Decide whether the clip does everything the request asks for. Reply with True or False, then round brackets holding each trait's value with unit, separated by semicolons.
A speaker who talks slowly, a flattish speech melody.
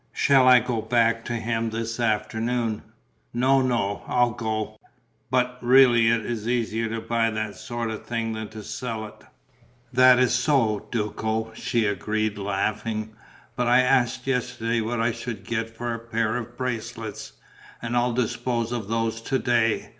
False (160 wpm; 1.8 semitones)